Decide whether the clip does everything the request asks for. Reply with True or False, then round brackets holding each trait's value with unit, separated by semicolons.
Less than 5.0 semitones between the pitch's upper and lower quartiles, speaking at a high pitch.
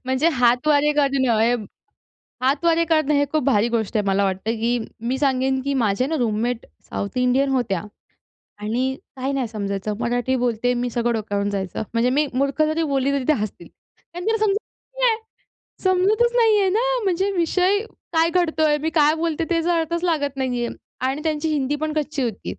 False (5.3 semitones; 275 Hz)